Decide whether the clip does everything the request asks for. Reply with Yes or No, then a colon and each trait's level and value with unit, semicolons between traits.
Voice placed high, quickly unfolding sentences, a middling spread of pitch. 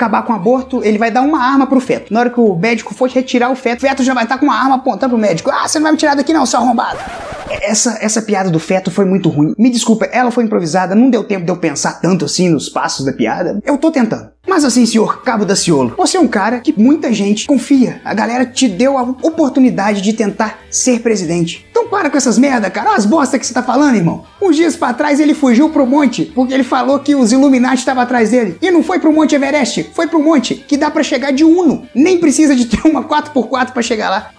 Yes: very high, 255 Hz; fast, 260 wpm; average, 4.4 semitones